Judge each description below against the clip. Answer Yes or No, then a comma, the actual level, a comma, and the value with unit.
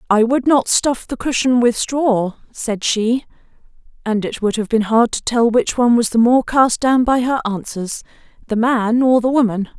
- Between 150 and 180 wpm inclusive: No, average, 200 wpm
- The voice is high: Yes, high, 235 Hz